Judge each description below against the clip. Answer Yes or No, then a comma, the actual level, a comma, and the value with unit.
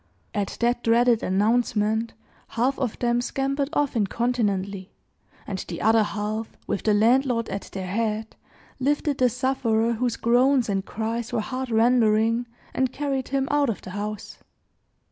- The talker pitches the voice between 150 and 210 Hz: No, high, 230 Hz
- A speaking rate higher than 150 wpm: No, average, 145 wpm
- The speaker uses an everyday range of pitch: Yes, average, 3.0 semitones